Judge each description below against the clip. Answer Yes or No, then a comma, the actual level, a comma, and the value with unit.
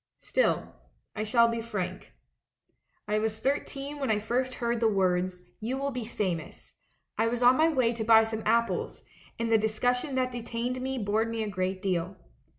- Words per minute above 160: Yes, average, 180 wpm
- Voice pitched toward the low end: No, high, 230 Hz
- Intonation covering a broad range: No, average, 2.8 semitones